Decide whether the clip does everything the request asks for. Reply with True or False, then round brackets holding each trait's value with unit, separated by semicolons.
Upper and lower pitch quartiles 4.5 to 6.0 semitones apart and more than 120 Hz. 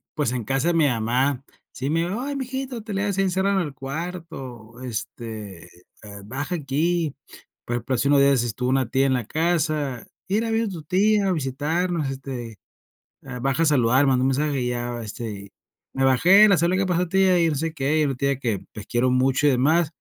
True (5.4 semitones; 140 Hz)